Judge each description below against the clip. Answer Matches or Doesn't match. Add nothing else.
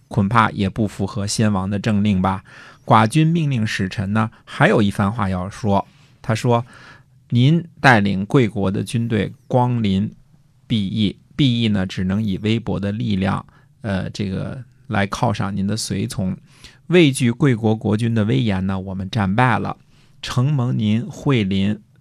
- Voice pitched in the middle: Doesn't match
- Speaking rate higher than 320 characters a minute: Doesn't match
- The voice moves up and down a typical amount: Matches